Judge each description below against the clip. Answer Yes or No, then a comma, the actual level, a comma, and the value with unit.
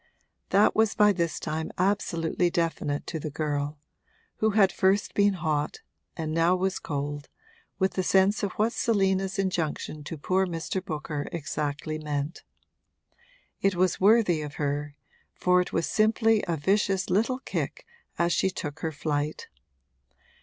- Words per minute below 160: Yes, average, 145 wpm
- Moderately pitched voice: Yes, medium, 175 Hz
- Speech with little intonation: No, average, 4.2 semitones